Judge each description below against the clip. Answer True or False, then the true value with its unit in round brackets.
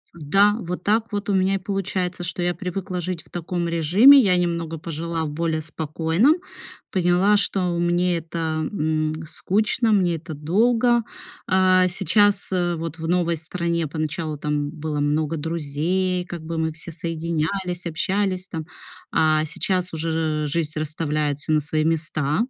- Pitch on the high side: False (170 Hz)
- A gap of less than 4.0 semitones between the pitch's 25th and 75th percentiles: True (2.8 semitones)